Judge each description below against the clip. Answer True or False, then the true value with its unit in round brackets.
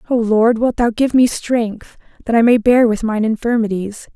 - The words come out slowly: False (200 wpm)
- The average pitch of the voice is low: False (230 Hz)